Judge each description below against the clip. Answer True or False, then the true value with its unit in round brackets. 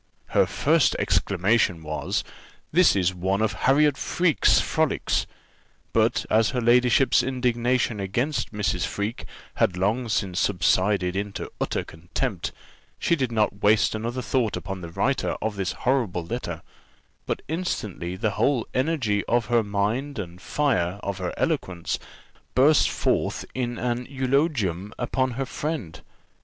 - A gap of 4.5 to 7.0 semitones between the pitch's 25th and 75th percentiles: True (5.1 semitones)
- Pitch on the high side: False (110 Hz)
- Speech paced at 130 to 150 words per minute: True (135 wpm)